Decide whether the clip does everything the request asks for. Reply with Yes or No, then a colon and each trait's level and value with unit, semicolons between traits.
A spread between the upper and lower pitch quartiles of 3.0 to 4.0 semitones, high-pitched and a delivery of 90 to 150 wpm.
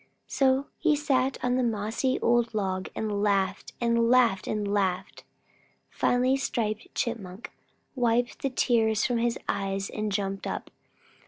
Yes: average, 3.6 semitones; high, 230 Hz; average, 140 wpm